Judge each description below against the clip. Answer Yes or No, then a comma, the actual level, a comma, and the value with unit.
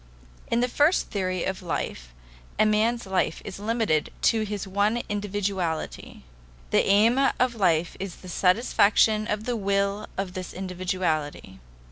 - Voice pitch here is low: No, high, 200 Hz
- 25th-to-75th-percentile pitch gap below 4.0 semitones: Yes, average, 2.8 semitones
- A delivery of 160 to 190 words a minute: No, average, 140 wpm